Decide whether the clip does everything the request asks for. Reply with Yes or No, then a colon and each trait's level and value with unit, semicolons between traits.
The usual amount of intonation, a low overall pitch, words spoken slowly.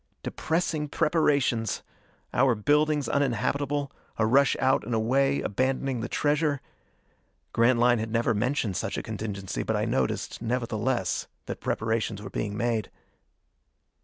Yes: average, 4.1 semitones; low, 125 Hz; slow, 125 wpm